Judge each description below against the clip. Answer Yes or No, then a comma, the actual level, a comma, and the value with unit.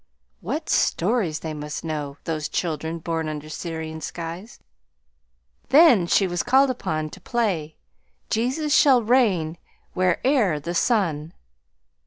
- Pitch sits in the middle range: Yes, medium, 170 Hz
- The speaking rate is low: Yes, slow, 120 wpm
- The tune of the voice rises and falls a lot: Yes, wide, 6.9 semitones